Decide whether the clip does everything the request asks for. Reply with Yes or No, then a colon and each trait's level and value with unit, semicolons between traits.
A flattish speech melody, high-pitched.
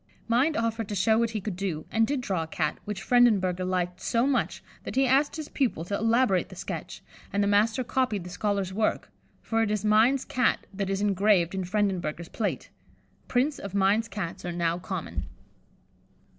No: average, 3.8 semitones; high, 205 Hz